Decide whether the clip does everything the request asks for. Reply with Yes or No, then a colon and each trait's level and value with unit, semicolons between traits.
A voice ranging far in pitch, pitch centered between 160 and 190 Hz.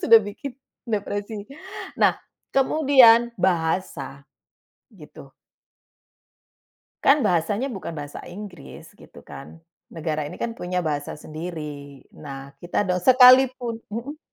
Yes: wide, 7.2 semitones; medium, 185 Hz